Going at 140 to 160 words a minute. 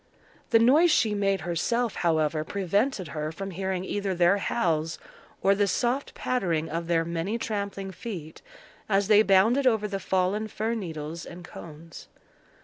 Yes: average, 150 wpm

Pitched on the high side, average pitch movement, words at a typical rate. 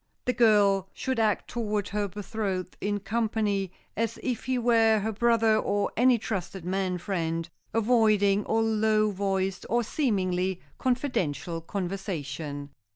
No: high, 205 Hz; average, 3.1 semitones; slow, 130 wpm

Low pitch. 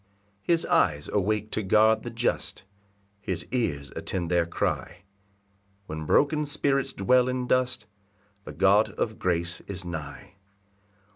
Yes: low, 105 Hz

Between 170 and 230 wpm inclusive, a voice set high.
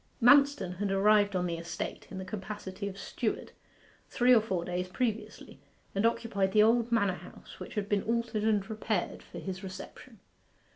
Yes: average, 175 wpm; high, 205 Hz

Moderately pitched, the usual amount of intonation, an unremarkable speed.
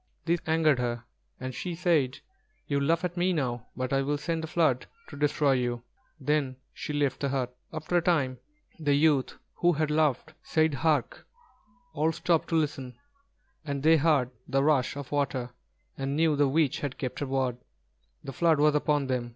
Yes: medium, 145 Hz; average, 3.1 semitones; average, 185 wpm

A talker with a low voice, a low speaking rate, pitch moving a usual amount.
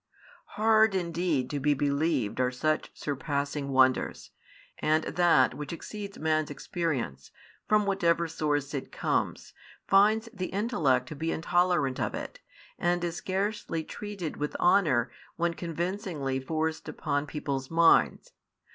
No: medium, 160 Hz; slow, 130 wpm; average, 4.0 semitones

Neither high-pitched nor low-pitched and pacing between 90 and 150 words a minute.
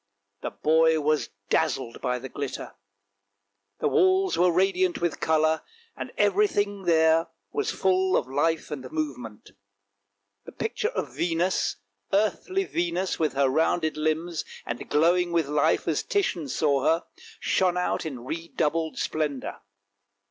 Yes: medium, 160 Hz; slow, 135 wpm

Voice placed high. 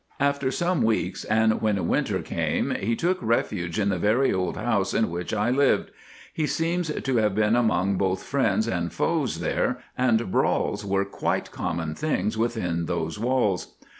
No: low, 110 Hz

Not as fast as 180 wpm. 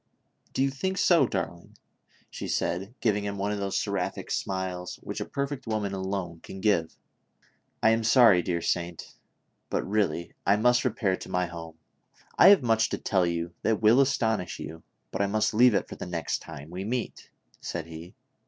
No: average, 190 wpm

